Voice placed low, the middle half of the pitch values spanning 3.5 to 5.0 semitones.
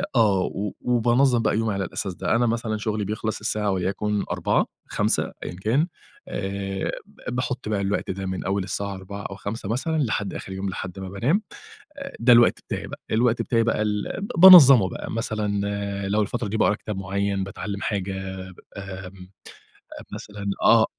No: low, 105 Hz; average, 2.8 semitones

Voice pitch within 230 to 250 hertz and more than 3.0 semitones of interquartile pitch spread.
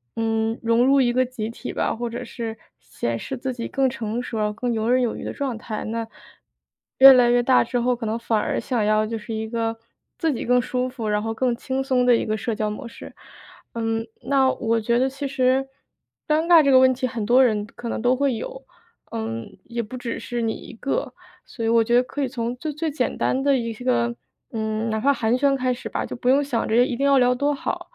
No: high, 240 Hz; narrow, 2.6 semitones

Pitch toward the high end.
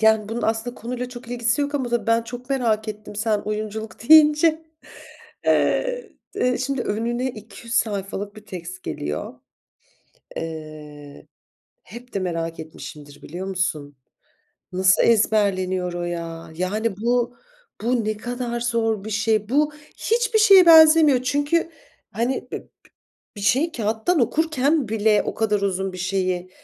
Yes: high, 220 Hz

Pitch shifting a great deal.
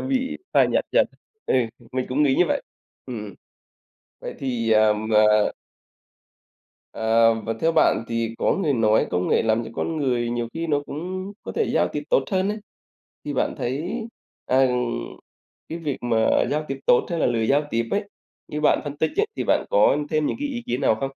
Yes: wide, 6.4 semitones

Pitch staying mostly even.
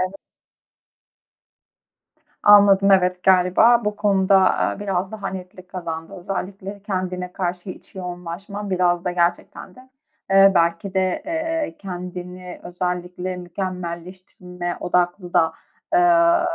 Yes: narrow, 1.7 semitones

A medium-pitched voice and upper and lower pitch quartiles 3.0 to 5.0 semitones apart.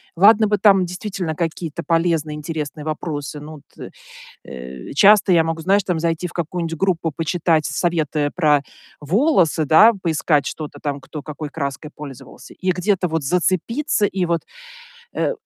Yes: medium, 165 Hz; average, 3.3 semitones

